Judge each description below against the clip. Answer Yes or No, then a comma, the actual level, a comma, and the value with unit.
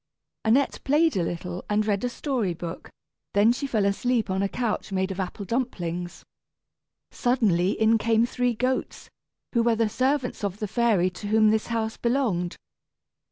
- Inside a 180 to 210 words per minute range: No, average, 165 wpm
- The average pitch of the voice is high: Yes, high, 220 Hz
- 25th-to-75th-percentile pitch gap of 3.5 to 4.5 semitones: Yes, average, 4.2 semitones